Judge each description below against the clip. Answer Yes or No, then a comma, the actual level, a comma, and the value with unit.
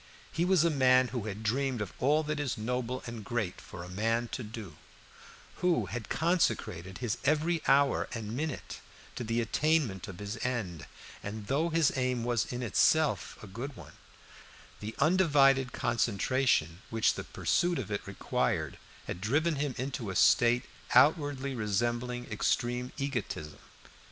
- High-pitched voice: No, low, 125 Hz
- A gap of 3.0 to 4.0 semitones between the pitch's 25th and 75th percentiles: No, average, 4.6 semitones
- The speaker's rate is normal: Yes, average, 150 wpm